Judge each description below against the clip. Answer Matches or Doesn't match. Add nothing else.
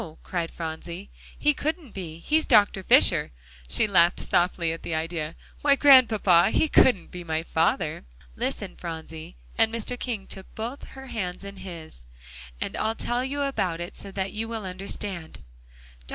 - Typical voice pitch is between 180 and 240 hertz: Matches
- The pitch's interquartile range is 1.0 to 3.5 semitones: Doesn't match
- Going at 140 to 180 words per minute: Matches